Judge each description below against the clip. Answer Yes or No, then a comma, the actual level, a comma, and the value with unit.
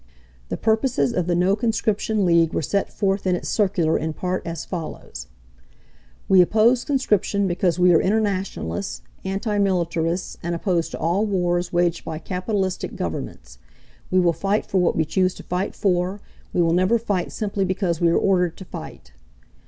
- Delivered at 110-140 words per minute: No, average, 170 wpm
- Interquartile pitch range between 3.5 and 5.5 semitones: No, average, 2.8 semitones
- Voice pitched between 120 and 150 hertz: No, medium, 185 Hz